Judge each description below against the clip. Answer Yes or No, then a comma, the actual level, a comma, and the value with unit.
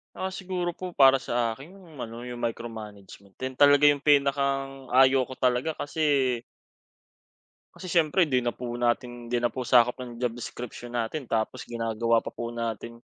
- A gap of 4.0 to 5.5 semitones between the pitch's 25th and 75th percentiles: No, average, 3.3 semitones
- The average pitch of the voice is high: No, low, 125 Hz